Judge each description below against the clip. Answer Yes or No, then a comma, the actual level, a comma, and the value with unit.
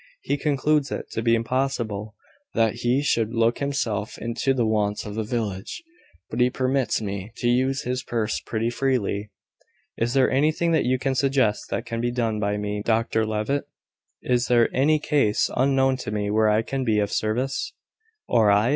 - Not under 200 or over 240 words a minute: No, average, 180 wpm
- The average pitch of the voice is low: Yes, low, 120 Hz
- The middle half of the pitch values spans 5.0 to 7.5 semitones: No, average, 3.6 semitones